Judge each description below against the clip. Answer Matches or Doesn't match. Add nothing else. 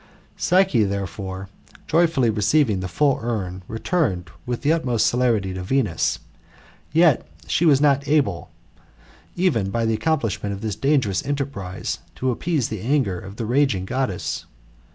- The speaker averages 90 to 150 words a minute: Matches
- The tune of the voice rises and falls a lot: Matches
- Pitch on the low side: Matches